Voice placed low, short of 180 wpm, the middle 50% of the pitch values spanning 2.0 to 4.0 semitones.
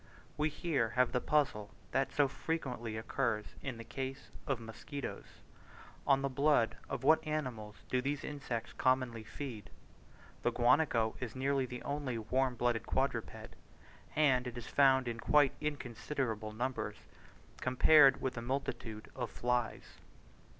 Yes: low, 130 Hz; average, 140 wpm; average, 3.3 semitones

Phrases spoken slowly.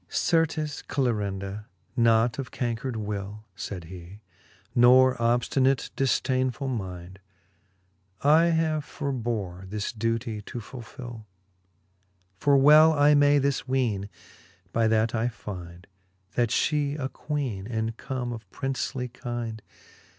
Yes: slow, 115 wpm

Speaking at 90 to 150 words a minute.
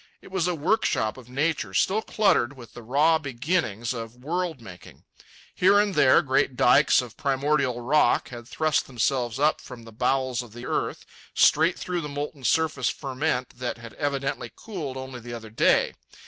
No: average, 170 wpm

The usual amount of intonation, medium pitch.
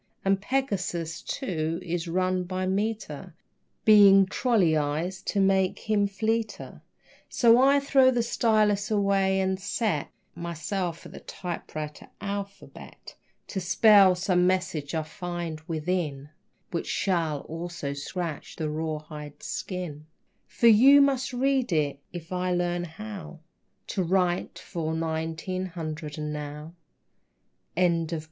Yes: average, 4.0 semitones; medium, 180 Hz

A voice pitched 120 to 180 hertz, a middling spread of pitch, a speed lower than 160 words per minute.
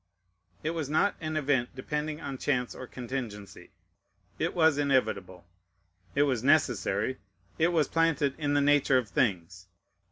Yes: low, 135 Hz; average, 3.9 semitones; average, 140 wpm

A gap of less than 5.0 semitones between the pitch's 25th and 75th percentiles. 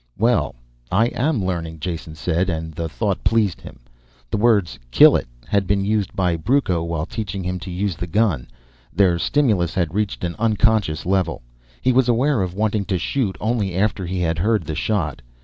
Yes: average, 4.2 semitones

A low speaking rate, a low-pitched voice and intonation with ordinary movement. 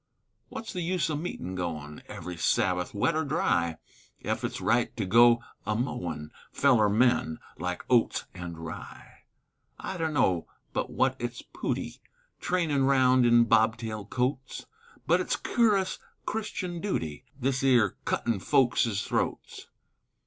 No: slow, 130 wpm; low, 120 Hz; wide, 7.7 semitones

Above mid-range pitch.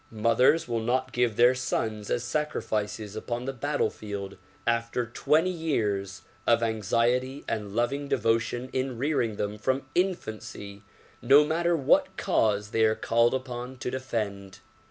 No: low, 120 Hz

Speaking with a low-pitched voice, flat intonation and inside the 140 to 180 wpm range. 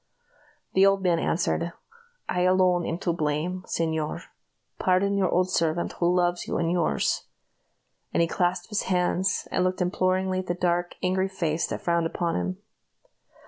No: medium, 180 Hz; narrow, 1.6 semitones; average, 165 wpm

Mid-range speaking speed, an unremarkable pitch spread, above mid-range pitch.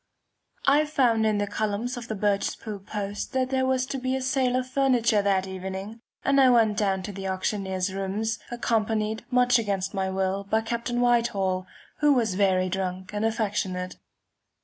Yes: average, 170 wpm; average, 4.1 semitones; high, 215 Hz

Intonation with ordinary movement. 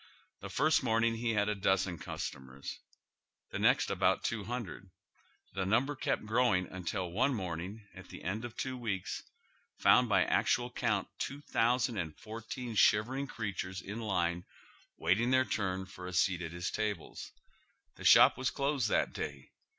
Yes: average, 4.7 semitones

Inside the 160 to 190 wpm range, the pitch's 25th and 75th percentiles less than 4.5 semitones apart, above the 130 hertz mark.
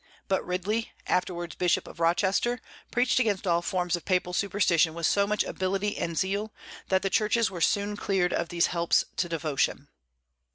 Yes: average, 170 wpm; average, 2.9 semitones; medium, 185 Hz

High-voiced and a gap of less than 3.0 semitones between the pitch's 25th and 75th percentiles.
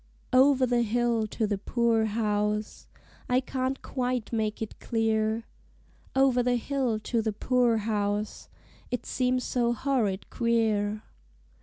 Yes: high, 230 Hz; narrow, 2.6 semitones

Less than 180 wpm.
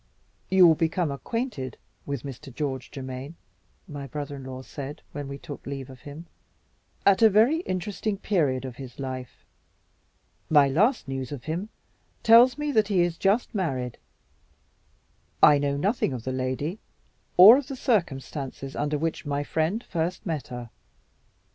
Yes: average, 160 wpm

